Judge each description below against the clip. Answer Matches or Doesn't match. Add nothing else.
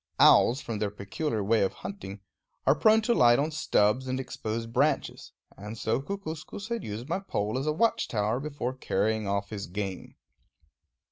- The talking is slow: Doesn't match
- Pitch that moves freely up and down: Matches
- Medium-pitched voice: Doesn't match